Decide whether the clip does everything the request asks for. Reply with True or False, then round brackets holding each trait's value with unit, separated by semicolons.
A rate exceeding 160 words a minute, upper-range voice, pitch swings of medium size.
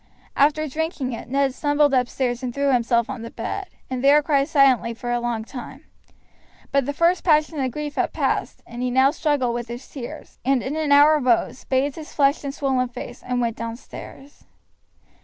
True (195 wpm; 270 Hz; 3.1 semitones)